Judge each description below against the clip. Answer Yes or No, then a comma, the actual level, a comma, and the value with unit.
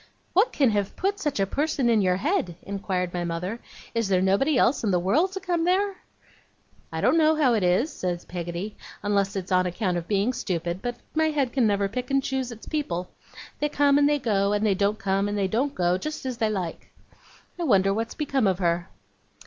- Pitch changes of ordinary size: No, wide, 7.1 semitones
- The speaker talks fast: Yes, fast, 220 wpm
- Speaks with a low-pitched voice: No, high, 210 Hz